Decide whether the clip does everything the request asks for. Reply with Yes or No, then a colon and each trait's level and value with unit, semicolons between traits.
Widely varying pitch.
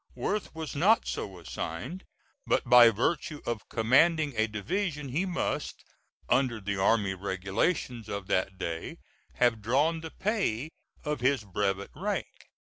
Yes: wide, 7.7 semitones